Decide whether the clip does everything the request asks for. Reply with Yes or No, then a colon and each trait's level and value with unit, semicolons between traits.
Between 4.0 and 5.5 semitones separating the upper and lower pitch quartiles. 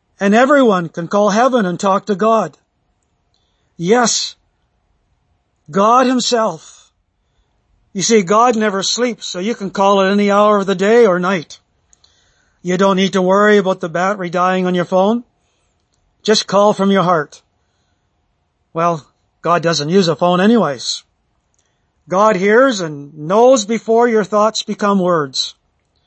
Yes: average, 5.0 semitones